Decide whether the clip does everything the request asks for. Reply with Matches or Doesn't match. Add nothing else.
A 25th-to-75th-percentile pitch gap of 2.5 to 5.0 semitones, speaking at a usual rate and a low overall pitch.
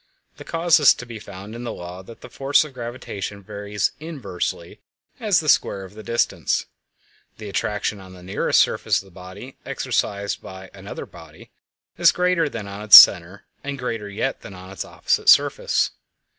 Matches